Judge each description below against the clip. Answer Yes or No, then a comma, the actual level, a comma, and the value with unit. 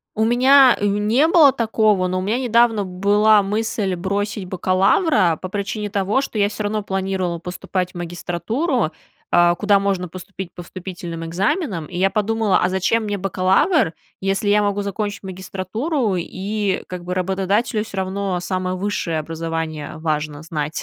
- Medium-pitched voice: No, high, 195 Hz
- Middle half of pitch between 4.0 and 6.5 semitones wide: No, average, 2.8 semitones